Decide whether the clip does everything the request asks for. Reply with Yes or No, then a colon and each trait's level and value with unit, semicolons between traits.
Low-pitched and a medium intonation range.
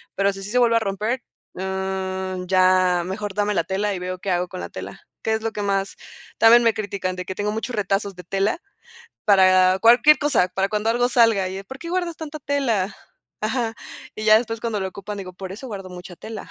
No: high, 200 Hz; average, 3.2 semitones